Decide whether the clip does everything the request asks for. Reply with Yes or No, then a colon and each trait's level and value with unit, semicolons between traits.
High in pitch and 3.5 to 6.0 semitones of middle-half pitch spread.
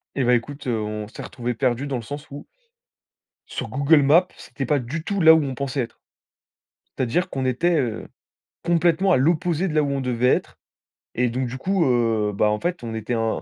No: low, 135 Hz; average, 4.9 semitones